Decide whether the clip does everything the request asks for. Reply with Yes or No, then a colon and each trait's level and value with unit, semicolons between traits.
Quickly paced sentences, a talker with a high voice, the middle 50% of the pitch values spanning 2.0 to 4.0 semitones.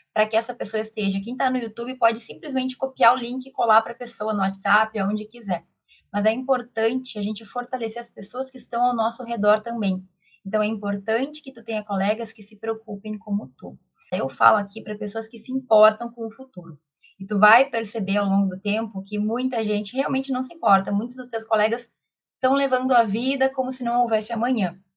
Yes: fast, 210 wpm; high, 225 Hz; average, 2.8 semitones